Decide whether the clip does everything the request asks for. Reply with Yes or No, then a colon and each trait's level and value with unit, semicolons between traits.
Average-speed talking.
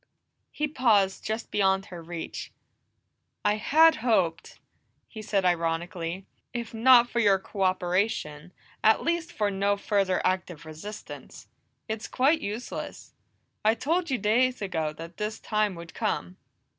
No: slow, 130 wpm